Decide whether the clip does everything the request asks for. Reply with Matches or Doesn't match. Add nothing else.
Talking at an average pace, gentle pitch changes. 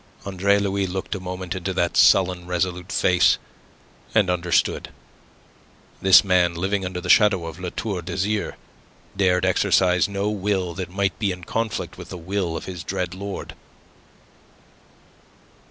Matches